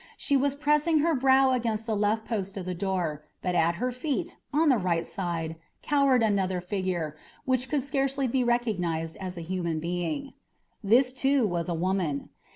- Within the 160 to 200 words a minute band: Yes, average, 175 wpm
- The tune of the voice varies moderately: No, wide, 7.0 semitones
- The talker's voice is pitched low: No, high, 210 Hz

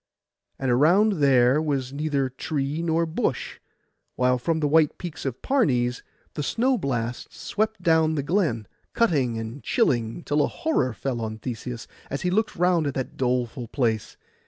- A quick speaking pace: No, average, 160 wpm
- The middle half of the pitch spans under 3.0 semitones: No, average, 5.1 semitones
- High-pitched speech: No, medium, 140 Hz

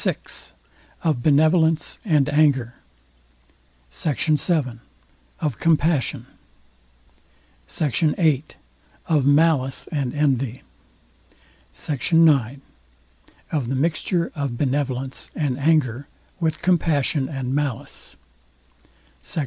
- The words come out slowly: Yes, slow, 90 wpm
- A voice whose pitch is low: No, medium, 145 Hz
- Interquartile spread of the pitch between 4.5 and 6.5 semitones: No, average, 3.2 semitones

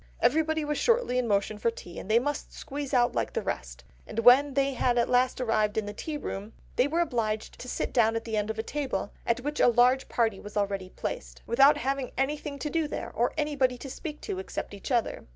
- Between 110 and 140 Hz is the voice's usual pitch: No, high, 245 Hz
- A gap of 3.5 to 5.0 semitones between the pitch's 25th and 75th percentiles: Yes, average, 4.6 semitones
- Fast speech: Yes, fast, 230 wpm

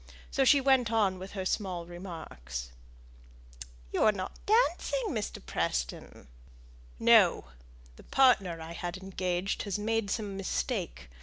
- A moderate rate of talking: No, slow, 130 wpm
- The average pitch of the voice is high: Yes, high, 195 Hz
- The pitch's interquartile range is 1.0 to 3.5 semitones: No, average, 4.5 semitones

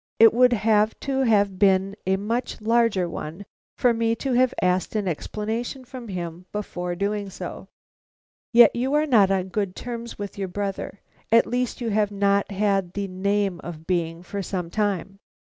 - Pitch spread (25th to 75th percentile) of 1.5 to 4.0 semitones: Yes, average, 3.4 semitones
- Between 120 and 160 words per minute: No, average, 175 wpm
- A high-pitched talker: Yes, high, 205 Hz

